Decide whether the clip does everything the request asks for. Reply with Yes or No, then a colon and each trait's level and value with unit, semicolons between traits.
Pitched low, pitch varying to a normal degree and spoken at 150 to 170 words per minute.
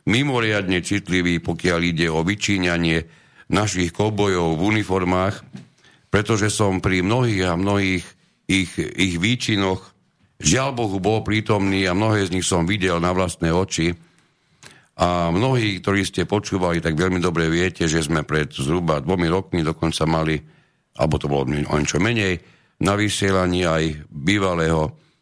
No: very low, 95 Hz; average, 3.1 semitones; average, 140 wpm